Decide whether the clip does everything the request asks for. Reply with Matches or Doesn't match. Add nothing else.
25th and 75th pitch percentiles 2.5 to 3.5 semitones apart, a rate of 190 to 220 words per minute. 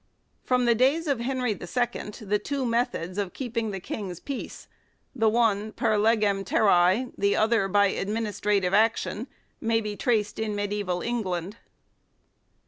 Doesn't match